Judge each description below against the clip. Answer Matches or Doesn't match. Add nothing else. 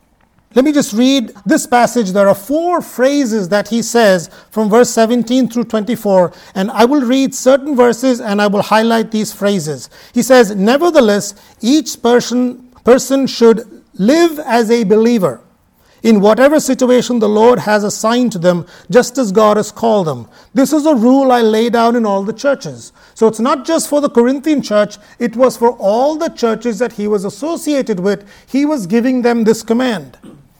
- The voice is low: Doesn't match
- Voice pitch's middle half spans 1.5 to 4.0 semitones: Matches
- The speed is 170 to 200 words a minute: Matches